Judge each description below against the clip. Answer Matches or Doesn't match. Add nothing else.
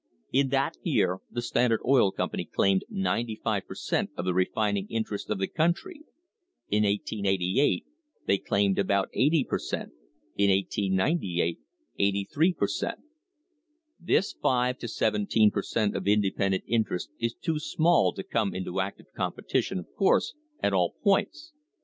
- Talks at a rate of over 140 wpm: Matches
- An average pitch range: Doesn't match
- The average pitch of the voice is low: Matches